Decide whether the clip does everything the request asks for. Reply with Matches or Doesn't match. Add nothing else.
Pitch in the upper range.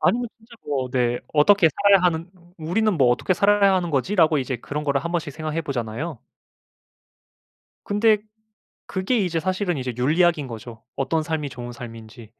Doesn't match